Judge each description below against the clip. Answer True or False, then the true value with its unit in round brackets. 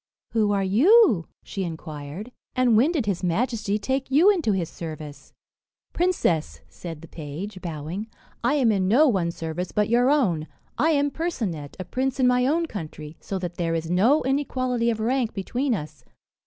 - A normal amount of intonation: False (7.6 semitones)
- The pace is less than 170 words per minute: False (175 wpm)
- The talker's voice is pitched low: False (210 Hz)